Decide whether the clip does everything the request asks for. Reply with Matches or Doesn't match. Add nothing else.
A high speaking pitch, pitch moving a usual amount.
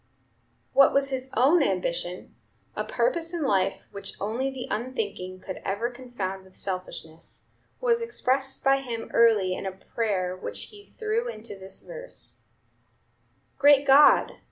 Doesn't match